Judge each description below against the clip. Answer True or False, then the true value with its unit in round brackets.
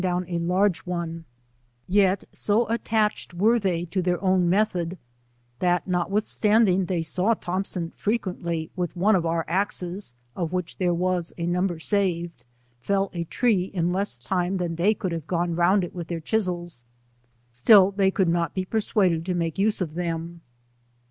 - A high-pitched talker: False (180 Hz)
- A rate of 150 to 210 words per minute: True (165 wpm)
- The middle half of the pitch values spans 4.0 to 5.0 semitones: False (2.5 semitones)